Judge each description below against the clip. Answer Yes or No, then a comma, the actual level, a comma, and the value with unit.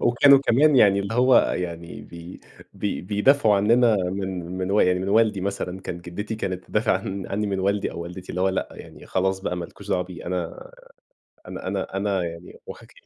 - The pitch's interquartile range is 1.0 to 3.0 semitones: Yes, average, 2.7 semitones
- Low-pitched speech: Yes, very low, 95 Hz